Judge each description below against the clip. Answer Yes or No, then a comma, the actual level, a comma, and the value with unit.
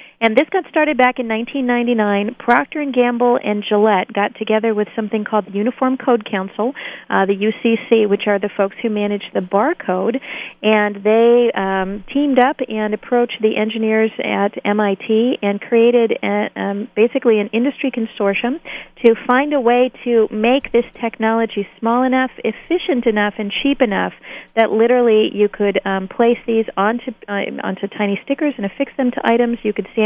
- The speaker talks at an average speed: Yes, average, 170 wpm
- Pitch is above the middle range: Yes, high, 225 Hz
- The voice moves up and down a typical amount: Yes, average, 3.0 semitones